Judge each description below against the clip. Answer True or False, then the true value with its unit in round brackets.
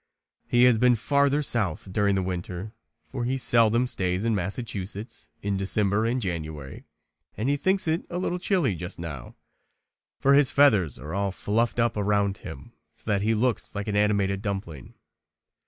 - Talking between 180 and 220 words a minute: False (170 wpm)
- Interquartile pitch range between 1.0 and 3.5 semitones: False (4.2 semitones)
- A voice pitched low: True (105 Hz)